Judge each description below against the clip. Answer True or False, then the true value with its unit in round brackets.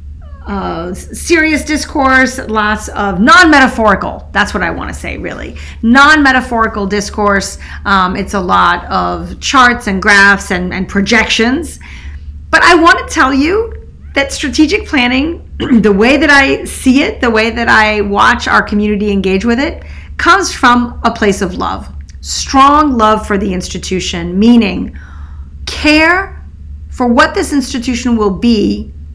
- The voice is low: False (220 Hz)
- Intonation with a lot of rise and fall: True (6.5 semitones)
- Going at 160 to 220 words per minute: False (150 wpm)